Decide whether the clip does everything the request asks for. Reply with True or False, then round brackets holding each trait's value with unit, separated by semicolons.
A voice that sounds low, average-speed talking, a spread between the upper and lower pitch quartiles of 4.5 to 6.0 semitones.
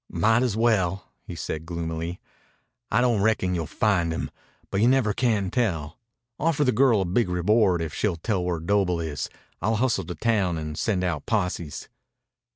True (95 Hz; 175 wpm; 4.9 semitones)